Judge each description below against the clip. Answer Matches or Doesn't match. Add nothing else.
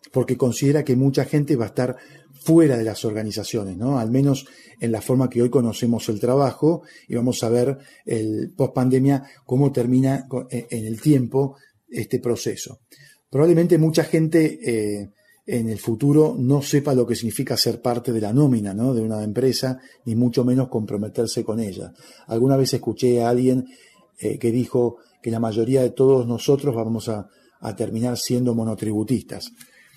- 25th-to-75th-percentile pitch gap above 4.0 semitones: Doesn't match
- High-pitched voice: Doesn't match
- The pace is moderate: Matches